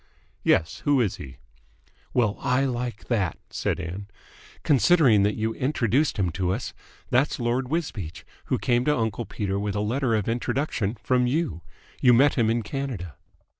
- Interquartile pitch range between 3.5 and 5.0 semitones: Yes, average, 4.4 semitones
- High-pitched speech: No, low, 120 Hz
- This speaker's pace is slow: No, average, 165 wpm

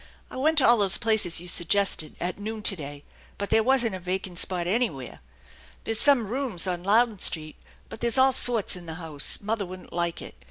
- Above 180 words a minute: Yes, fast, 205 wpm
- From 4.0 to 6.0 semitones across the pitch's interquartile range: Yes, average, 4.7 semitones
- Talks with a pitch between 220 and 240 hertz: No, high, 200 Hz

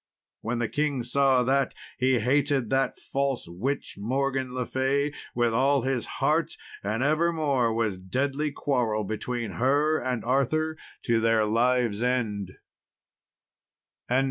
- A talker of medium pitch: No, low, 125 Hz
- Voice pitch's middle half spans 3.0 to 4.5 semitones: Yes, average, 3.3 semitones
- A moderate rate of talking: No, slow, 125 wpm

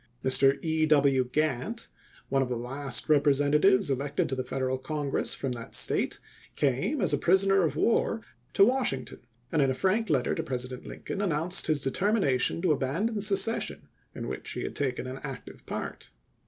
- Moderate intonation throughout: No, wide, 6.2 semitones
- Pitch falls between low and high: Yes, medium, 145 Hz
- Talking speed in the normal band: Yes, average, 180 wpm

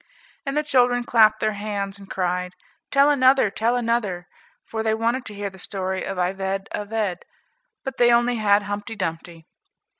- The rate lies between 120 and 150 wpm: No, average, 170 wpm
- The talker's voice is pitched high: Yes, high, 210 Hz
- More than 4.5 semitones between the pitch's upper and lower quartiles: No, average, 3.7 semitones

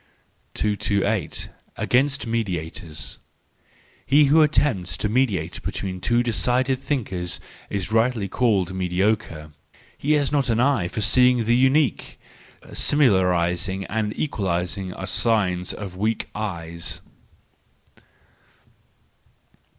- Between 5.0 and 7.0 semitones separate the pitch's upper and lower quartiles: Yes, wide, 5.4 semitones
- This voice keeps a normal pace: No, slow, 100 wpm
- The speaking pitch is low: Yes, low, 105 Hz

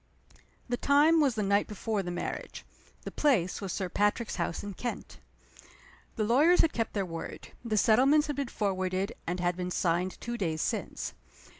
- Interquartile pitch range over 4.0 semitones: Yes, average, 5.2 semitones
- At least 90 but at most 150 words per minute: No, average, 175 wpm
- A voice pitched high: Yes, high, 210 Hz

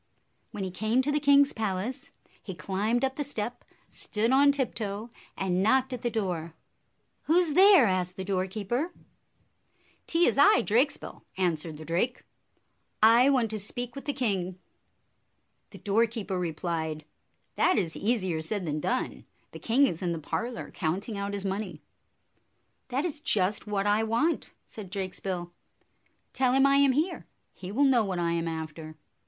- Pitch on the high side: Yes, high, 210 Hz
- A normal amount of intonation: No, wide, 5.9 semitones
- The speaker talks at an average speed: Yes, average, 160 wpm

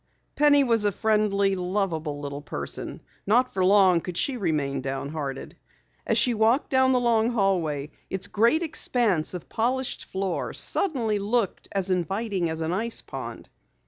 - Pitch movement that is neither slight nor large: No, wide, 5.7 semitones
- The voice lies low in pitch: No, high, 195 Hz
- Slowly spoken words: No, average, 150 wpm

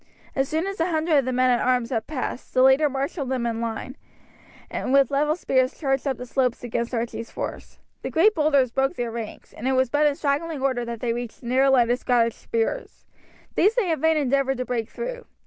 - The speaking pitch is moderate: No, very high, 265 Hz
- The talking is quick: Yes, fast, 230 wpm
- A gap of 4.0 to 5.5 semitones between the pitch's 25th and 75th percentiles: No, average, 3.5 semitones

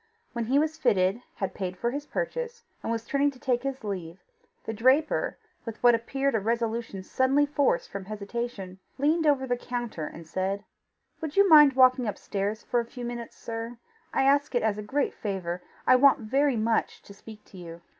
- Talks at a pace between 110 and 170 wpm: No, average, 195 wpm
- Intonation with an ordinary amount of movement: Yes, average, 5.0 semitones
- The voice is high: Yes, high, 235 Hz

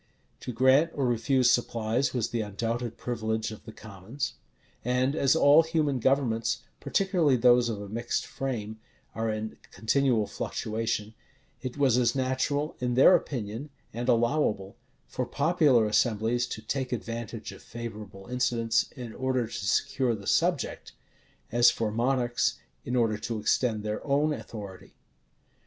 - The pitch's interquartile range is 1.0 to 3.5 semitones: Yes, average, 3.1 semitones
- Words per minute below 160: Yes, average, 145 wpm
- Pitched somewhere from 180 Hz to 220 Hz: No, low, 120 Hz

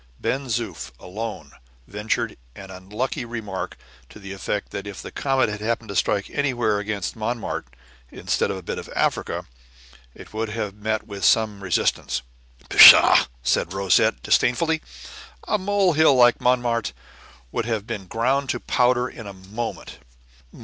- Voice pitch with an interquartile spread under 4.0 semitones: Yes, average, 3.5 semitones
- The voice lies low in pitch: Yes, low, 110 Hz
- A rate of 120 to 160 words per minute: Yes, average, 150 wpm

